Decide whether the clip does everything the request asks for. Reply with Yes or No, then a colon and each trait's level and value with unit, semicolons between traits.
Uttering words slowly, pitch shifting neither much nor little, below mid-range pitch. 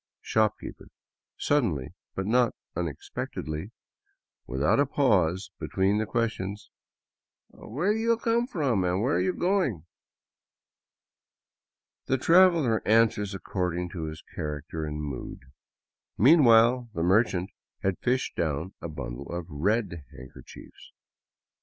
No: slow, 120 wpm; wide, 7.2 semitones; low, 100 Hz